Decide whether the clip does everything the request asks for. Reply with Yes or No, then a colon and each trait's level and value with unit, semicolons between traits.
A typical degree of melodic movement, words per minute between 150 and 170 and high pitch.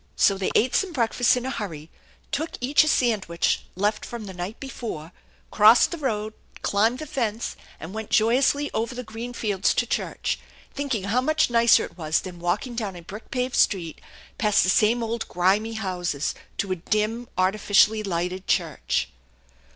No: average, 4.4 semitones; average, 180 wpm; high, 215 Hz